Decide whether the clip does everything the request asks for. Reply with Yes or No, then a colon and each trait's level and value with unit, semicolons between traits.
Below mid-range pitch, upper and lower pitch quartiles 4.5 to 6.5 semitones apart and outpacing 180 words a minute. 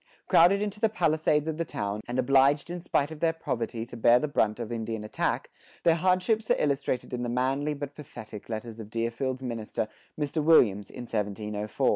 Yes: low, 130 Hz; wide, 5.6 semitones; average, 190 wpm